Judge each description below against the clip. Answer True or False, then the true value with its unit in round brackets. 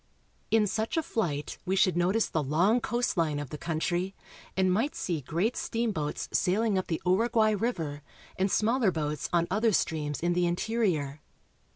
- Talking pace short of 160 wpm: False (170 wpm)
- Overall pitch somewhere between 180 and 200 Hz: True (185 Hz)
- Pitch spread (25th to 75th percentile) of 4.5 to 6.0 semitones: True (5.6 semitones)